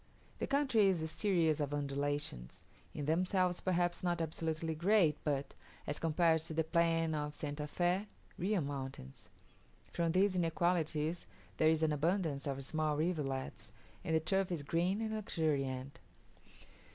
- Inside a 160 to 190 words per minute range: No, average, 145 wpm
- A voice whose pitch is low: No, medium, 160 Hz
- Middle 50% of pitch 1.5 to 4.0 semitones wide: Yes, average, 3.3 semitones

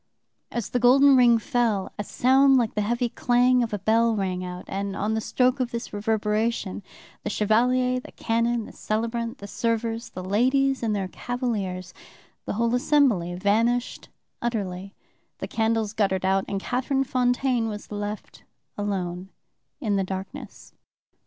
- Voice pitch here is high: Yes, high, 225 Hz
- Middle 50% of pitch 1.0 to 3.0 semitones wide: No, average, 3.5 semitones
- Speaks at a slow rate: No, average, 150 wpm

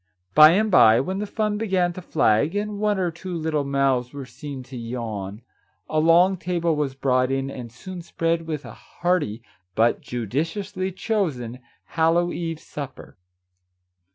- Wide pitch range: Yes, wide, 6.1 semitones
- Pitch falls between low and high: Yes, medium, 160 Hz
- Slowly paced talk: No, average, 155 wpm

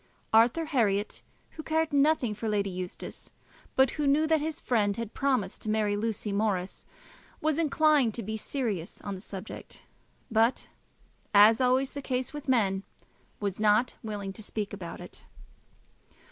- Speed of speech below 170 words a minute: Yes, average, 160 wpm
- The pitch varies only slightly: No, average, 5.3 semitones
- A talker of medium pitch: No, high, 225 Hz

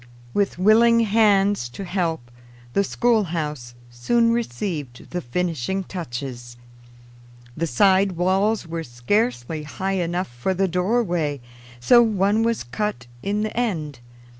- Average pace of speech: No, slow, 120 wpm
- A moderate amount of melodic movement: No, wide, 6.0 semitones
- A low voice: No, medium, 180 Hz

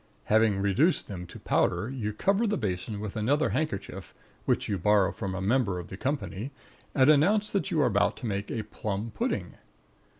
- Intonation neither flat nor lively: No, wide, 5.8 semitones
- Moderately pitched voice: No, low, 105 Hz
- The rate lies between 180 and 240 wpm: Yes, average, 190 wpm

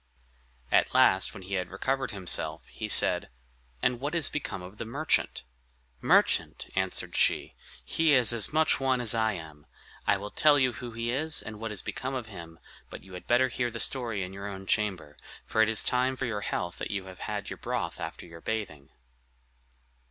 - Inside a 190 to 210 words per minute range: Yes, average, 195 wpm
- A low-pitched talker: Yes, low, 110 Hz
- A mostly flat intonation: No, average, 5.1 semitones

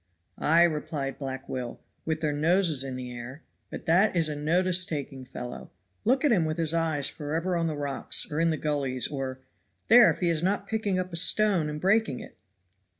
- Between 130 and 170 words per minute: No, fast, 205 wpm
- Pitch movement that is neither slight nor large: Yes, average, 4.6 semitones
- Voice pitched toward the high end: No, medium, 160 Hz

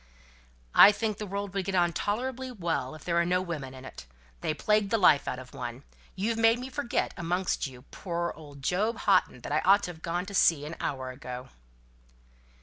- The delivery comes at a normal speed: No, fast, 210 wpm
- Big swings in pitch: Yes, wide, 6.1 semitones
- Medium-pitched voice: Yes, medium, 175 Hz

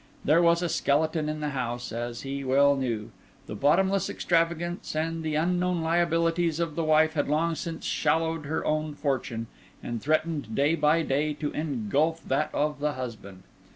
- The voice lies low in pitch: No, medium, 155 Hz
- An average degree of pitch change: Yes, average, 3.0 semitones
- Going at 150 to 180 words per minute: Yes, average, 170 wpm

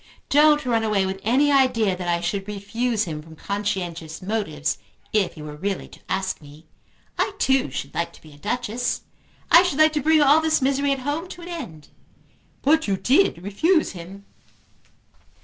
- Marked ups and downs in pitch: Yes, wide, 8.1 semitones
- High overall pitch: Yes, high, 210 Hz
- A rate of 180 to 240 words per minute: Yes, average, 185 wpm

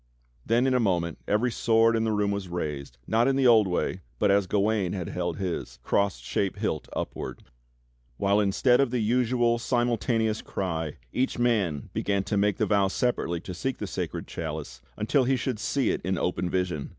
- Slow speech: No, average, 195 wpm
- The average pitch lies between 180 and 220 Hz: No, low, 105 Hz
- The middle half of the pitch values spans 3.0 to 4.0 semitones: No, average, 4.6 semitones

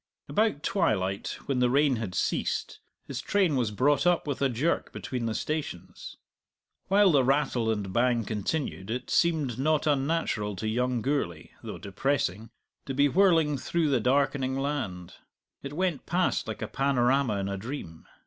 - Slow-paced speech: No, average, 160 wpm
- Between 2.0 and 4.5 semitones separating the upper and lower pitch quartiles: No, average, 5.0 semitones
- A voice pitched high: No, low, 135 Hz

